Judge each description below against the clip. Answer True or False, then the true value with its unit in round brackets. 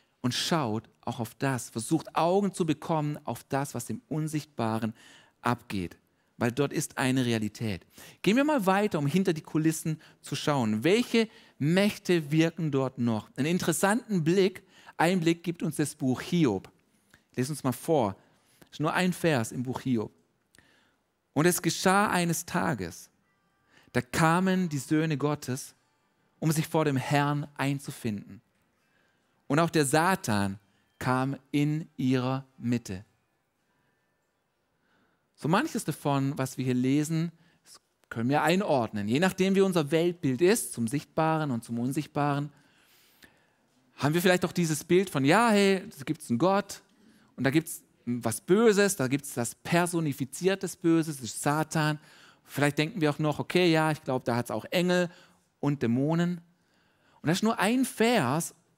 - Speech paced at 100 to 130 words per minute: False (155 wpm)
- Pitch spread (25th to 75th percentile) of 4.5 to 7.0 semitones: True (5.0 semitones)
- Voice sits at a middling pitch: True (150 Hz)